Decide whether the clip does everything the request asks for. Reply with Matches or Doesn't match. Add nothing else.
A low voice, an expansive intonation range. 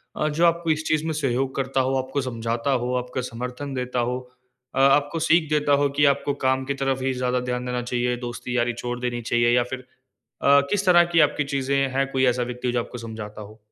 Doesn't match